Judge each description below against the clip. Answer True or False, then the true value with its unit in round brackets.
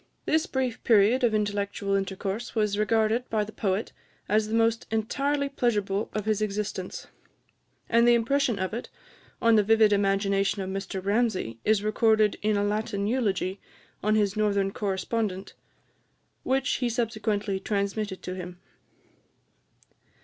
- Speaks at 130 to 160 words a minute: True (140 wpm)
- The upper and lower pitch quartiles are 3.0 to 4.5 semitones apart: False (2.4 semitones)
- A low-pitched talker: False (215 Hz)